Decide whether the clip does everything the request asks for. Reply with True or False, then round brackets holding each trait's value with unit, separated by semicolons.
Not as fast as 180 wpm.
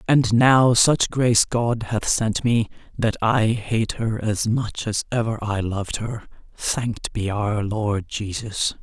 True (165 wpm)